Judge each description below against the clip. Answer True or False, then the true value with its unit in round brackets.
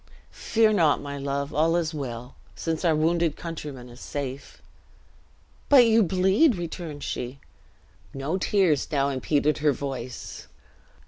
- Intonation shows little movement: False (3.9 semitones)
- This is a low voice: False (150 Hz)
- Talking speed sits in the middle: False (130 wpm)